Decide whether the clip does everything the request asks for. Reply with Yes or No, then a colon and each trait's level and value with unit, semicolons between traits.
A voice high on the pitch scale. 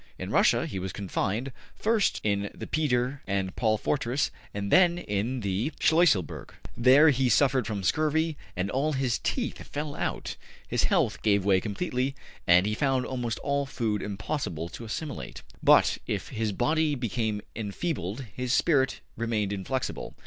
No: low, 120 Hz